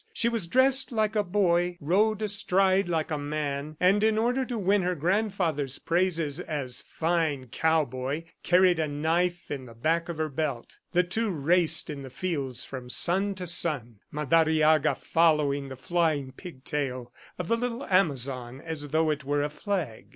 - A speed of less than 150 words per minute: No, average, 165 wpm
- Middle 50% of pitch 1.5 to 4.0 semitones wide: No, average, 4.5 semitones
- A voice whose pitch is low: No, medium, 160 Hz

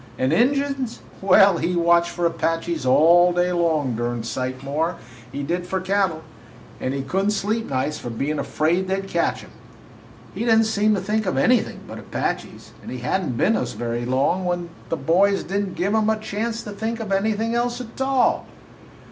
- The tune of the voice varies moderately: No, wide, 5.7 semitones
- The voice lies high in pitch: No, medium, 180 Hz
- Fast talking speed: Yes, fast, 210 wpm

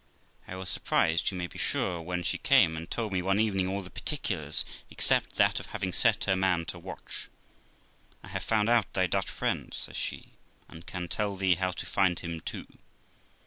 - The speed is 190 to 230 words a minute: Yes, average, 200 wpm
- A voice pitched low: Yes, very low, 95 Hz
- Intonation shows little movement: Yes, narrow, 2.0 semitones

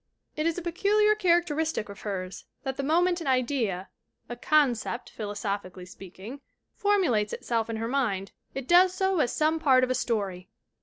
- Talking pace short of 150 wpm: No, average, 170 wpm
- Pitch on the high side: Yes, very high, 255 Hz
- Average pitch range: No, wide, 8.1 semitones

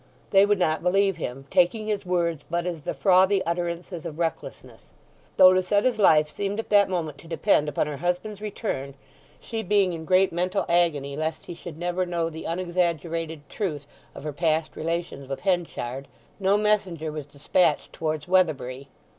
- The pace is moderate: Yes, average, 170 wpm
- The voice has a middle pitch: Yes, medium, 175 Hz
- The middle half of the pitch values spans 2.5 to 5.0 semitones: Yes, average, 3.3 semitones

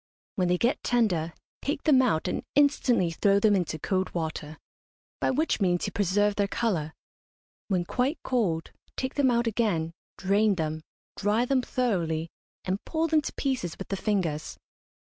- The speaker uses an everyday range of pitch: No, wide, 6.2 semitones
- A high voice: Yes, high, 200 Hz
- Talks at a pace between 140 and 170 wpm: Yes, average, 165 wpm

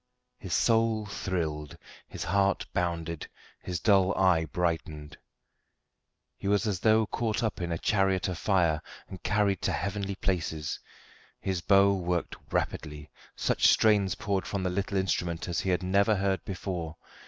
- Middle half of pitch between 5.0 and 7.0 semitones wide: No, average, 2.8 semitones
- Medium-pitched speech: No, very low, 95 Hz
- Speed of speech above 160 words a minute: No, average, 150 wpm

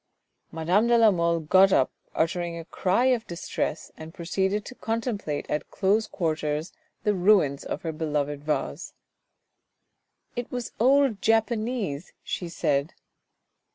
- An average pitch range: No, wide, 5.8 semitones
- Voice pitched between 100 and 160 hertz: No, medium, 180 Hz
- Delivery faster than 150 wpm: No, slow, 135 wpm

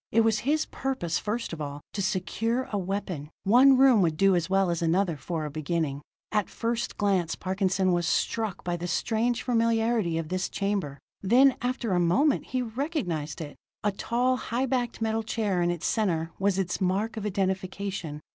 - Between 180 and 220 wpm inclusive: Yes, average, 185 wpm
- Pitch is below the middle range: No, high, 195 Hz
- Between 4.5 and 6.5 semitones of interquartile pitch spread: Yes, average, 4.9 semitones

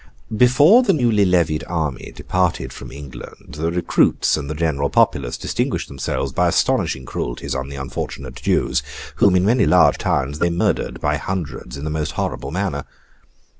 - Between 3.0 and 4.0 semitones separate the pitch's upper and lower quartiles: No, average, 5.0 semitones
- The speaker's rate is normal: Yes, average, 165 wpm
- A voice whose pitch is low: Yes, very low, 75 Hz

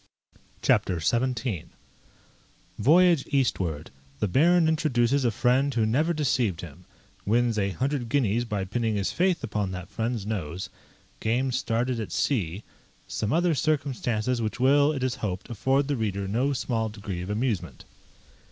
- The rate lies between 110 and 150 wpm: Yes, average, 145 wpm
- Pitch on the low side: Yes, low, 120 Hz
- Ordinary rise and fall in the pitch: Yes, average, 4.8 semitones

